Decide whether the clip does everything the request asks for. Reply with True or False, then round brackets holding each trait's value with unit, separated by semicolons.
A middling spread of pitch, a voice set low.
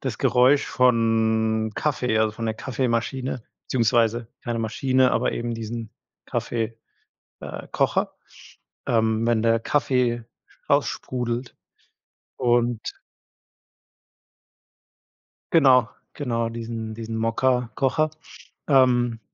False (2.1 semitones; 115 Hz)